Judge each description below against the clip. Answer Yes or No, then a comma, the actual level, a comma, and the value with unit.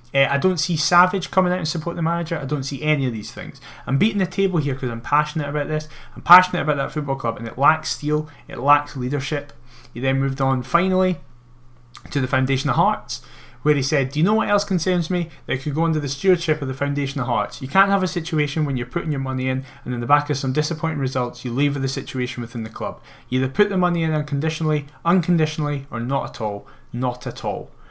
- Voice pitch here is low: No, medium, 145 Hz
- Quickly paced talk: Yes, fast, 245 wpm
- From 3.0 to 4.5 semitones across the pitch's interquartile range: Yes, average, 4.2 semitones